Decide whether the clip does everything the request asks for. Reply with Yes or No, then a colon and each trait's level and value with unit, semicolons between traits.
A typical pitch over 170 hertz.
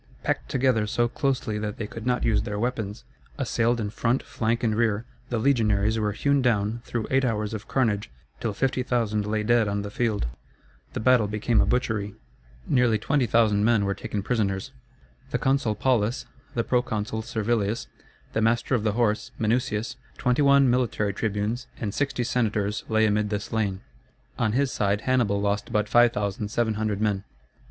No: low, 110 Hz